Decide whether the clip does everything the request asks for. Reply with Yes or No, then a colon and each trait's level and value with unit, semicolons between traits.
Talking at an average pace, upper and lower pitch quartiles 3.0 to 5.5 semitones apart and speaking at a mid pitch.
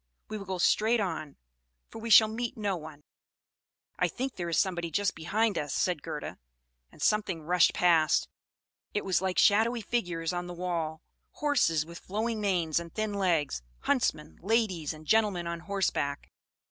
Yes: average, 165 wpm; average, 4.5 semitones; medium, 180 Hz